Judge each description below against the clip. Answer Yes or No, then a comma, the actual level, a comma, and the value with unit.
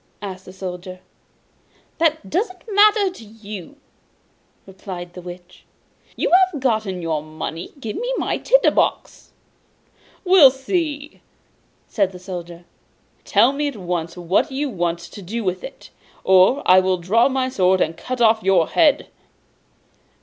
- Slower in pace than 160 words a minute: Yes, average, 140 wpm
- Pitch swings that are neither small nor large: No, wide, 7.7 semitones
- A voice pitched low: No, high, 200 Hz